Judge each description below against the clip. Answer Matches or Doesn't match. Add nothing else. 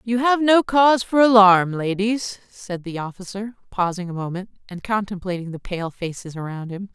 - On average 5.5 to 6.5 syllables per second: Doesn't match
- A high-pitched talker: Matches